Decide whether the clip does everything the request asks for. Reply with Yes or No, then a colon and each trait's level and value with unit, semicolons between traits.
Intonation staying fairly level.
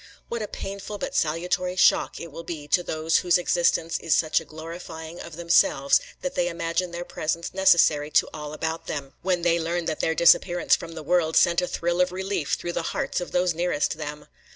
Yes: narrow, 1.9 semitones